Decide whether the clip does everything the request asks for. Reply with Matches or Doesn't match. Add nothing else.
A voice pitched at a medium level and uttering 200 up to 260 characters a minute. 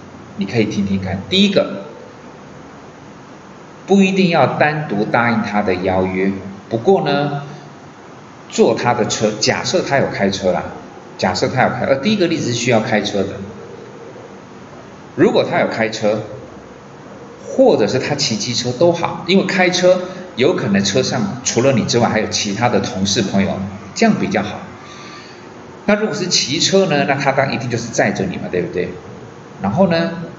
Doesn't match